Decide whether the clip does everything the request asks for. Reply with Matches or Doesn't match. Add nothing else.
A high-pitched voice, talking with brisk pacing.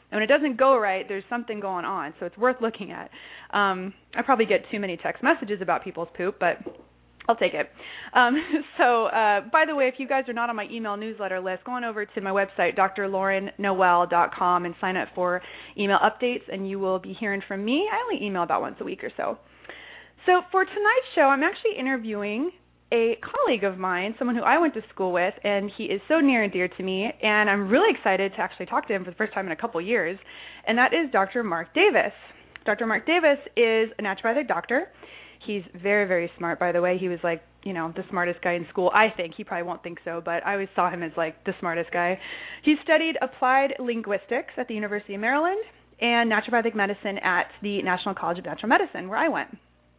Matches